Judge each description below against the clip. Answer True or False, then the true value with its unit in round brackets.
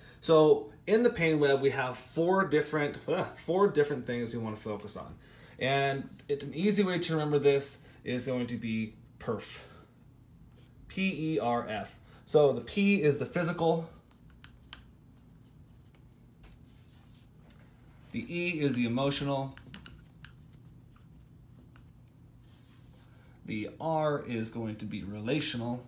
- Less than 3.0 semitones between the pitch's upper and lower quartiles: False (3.8 semitones)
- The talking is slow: True (125 wpm)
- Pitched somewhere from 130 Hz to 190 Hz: True (140 Hz)